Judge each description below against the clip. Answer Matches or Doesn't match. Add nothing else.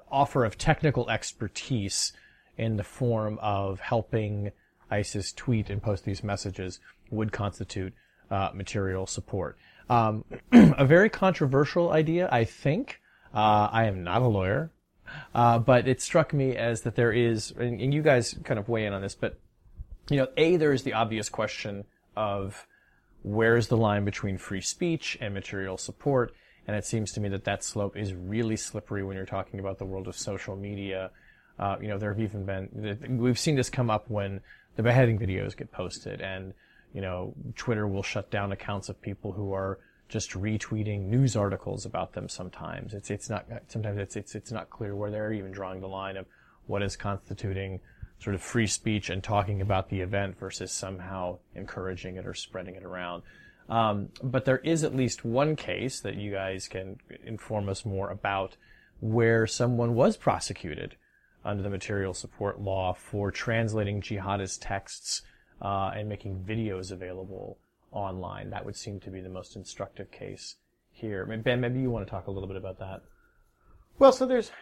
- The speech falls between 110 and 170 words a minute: Doesn't match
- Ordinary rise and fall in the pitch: Matches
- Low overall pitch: Matches